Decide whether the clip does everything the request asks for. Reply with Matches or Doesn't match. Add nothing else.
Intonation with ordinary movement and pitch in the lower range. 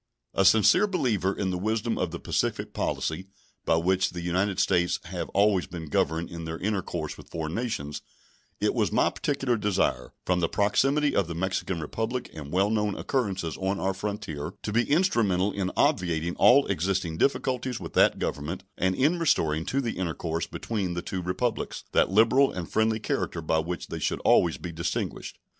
Matches